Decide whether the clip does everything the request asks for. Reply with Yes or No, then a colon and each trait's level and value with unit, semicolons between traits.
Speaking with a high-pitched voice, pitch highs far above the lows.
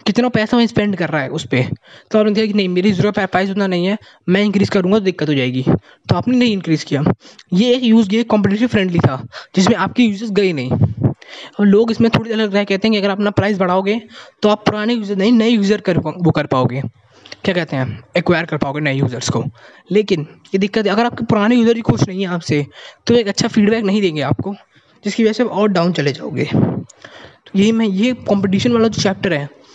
Yes: high, 200 Hz; wide, 5.8 semitones